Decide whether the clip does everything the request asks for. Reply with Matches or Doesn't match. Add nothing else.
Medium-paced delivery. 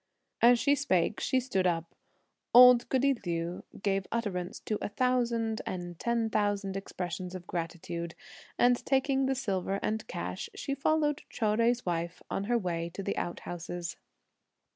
Matches